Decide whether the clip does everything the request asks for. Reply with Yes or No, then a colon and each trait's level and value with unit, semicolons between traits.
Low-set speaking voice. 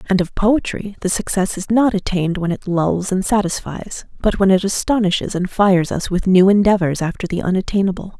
No: high, 190 Hz